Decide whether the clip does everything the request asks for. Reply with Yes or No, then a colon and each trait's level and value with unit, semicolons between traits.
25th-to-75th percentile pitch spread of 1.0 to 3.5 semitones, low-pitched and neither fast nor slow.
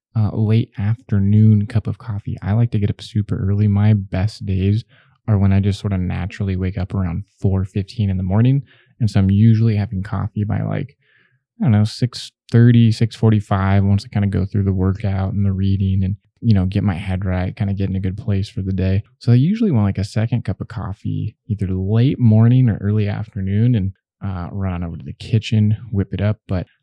No: narrow, 2.6 semitones; low, 105 Hz; fast, 225 wpm